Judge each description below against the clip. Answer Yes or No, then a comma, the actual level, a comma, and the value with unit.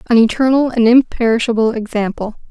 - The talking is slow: Yes, slow, 120 wpm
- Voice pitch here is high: Yes, high, 235 Hz